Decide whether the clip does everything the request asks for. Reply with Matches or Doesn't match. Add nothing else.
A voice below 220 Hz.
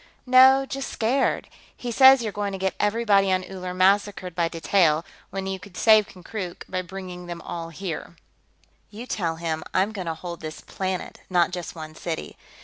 Matches